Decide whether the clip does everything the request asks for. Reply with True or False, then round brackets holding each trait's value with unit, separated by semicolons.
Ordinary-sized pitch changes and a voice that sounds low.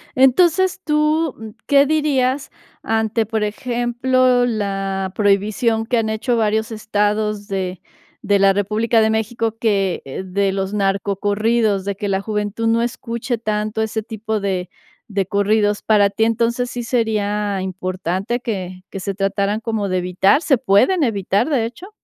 False (3.0 semitones; 215 Hz)